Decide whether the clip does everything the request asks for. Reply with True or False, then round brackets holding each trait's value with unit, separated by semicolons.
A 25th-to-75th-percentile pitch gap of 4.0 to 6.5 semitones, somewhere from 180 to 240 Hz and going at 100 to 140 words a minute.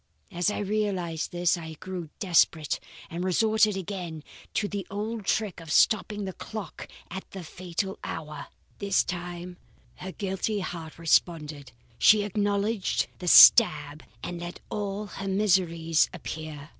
False (3.4 semitones; 185 Hz; 135 wpm)